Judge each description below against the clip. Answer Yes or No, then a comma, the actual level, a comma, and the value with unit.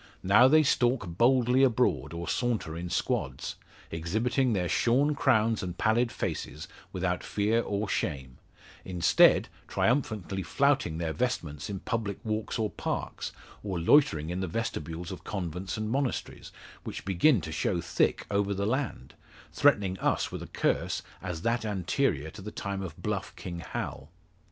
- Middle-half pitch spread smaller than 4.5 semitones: No, wide, 5.4 semitones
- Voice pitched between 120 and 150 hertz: No, low, 100 Hz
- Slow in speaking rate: No, average, 150 wpm